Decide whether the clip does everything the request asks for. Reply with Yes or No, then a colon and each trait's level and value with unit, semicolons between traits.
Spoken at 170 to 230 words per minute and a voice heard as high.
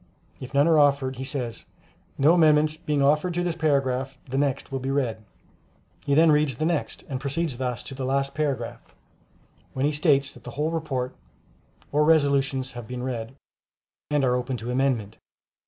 No: average, 180 wpm; medium, 140 Hz